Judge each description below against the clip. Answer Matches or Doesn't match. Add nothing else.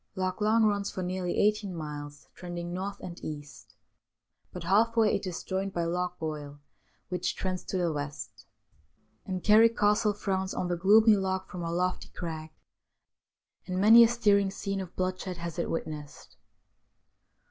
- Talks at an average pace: Matches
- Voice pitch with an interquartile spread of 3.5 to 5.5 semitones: Doesn't match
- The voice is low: Doesn't match